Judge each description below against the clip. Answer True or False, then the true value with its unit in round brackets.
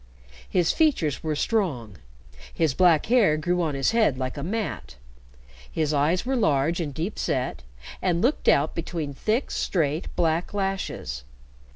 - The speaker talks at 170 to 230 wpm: False (150 wpm)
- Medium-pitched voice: True (165 Hz)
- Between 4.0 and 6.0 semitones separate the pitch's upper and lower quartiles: True (5.1 semitones)